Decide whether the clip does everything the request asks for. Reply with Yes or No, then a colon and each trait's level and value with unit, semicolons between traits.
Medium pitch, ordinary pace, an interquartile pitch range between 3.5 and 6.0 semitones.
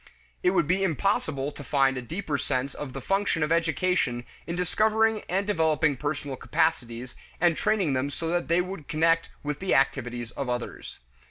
Yes: medium, 155 Hz; average, 175 wpm; average, 5.0 semitones